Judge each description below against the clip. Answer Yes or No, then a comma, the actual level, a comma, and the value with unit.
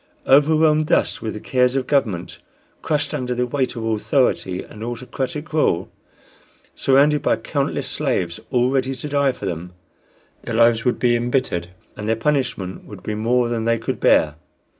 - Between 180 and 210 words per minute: No, average, 165 wpm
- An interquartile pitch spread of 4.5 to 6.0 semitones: No, average, 3.9 semitones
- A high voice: No, low, 125 Hz